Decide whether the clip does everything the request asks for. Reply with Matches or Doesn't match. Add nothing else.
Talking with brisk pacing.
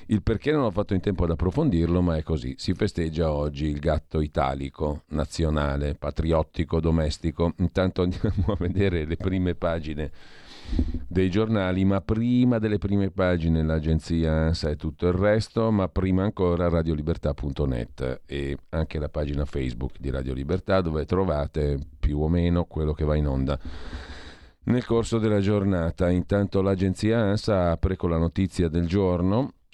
Doesn't match